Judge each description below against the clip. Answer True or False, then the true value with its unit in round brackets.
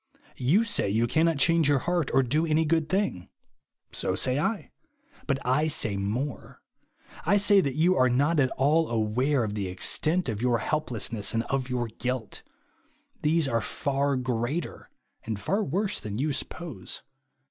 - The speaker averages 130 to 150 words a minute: False (165 wpm)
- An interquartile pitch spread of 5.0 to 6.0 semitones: True (5.5 semitones)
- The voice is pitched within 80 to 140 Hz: True (135 Hz)